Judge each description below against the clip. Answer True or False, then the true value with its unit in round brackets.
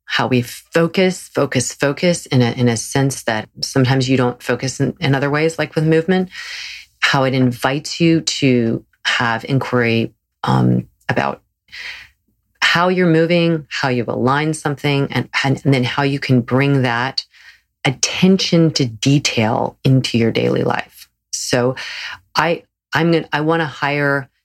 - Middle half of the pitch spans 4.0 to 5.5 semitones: True (4.3 semitones)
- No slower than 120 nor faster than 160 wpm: True (150 wpm)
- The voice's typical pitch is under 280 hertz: True (135 Hz)